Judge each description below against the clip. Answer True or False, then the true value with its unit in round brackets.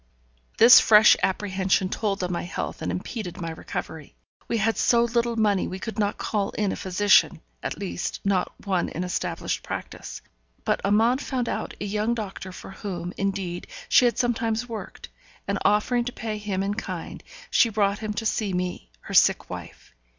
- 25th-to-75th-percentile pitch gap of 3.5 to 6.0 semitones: False (3.1 semitones)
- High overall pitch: True (205 Hz)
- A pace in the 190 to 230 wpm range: False (180 wpm)